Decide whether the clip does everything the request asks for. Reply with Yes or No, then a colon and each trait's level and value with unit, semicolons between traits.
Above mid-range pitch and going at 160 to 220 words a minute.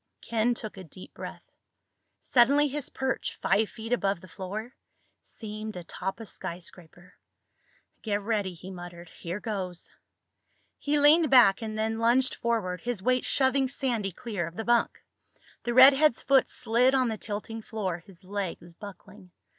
No: high, 220 Hz; average, 150 wpm